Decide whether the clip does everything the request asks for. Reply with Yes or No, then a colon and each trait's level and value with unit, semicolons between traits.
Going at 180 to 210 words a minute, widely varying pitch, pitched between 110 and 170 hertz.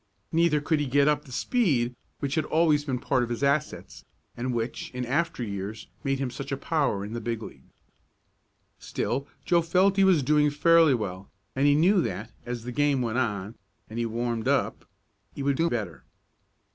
No: average, 195 wpm; average, 4.3 semitones; low, 135 Hz